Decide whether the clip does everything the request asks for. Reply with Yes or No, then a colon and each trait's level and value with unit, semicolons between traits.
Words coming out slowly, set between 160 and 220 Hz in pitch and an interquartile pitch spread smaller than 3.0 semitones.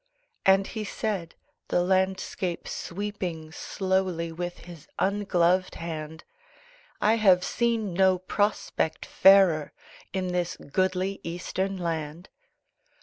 Yes: slow, 100 wpm; medium, 185 Hz; narrow, 2.4 semitones